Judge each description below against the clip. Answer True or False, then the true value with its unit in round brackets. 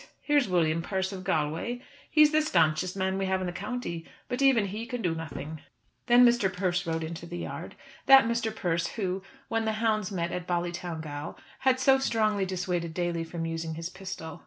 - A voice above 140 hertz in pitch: True (185 Hz)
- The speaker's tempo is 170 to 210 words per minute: True (190 wpm)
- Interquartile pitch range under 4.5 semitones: False (5.1 semitones)